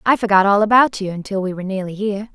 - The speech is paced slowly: No, fast, 255 wpm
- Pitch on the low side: No, high, 200 Hz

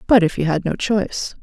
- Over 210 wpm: Yes, fast, 255 wpm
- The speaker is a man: No, female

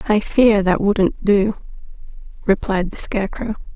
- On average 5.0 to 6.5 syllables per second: No, 4.4 syllables/s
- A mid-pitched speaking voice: No, high, 205 Hz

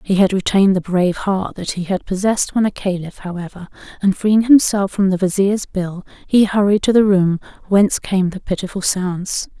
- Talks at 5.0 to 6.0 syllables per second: Yes, 5.2 syllables/s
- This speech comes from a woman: Yes, female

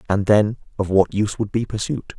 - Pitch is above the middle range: No, low, 105 Hz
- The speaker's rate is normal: No, fast, 220 wpm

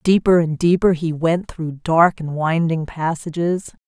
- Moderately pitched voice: Yes, medium, 165 Hz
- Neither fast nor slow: Yes, average, 155 wpm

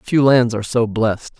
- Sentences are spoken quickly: Yes, fast, 215 wpm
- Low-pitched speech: Yes, low, 120 Hz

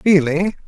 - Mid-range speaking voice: Yes, medium, 175 Hz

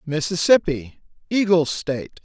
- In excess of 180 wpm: No, slow, 80 wpm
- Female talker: No, male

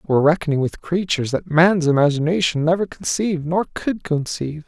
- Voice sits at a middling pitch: Yes, medium, 160 Hz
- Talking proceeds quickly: No, average, 140 wpm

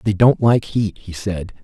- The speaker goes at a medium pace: No, fast, 220 wpm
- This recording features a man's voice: Yes, male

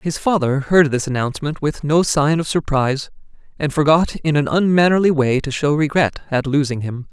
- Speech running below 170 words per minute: No, average, 185 wpm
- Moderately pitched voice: Yes, medium, 150 Hz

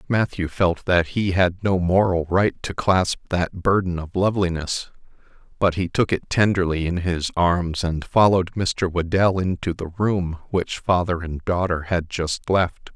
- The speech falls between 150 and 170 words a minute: Yes, average, 165 wpm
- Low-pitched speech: Yes, very low, 90 Hz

